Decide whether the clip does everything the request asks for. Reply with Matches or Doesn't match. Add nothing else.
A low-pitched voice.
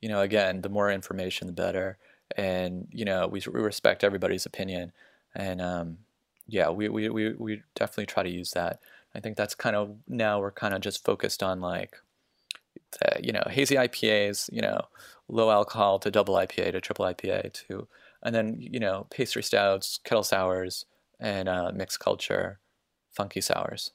Matches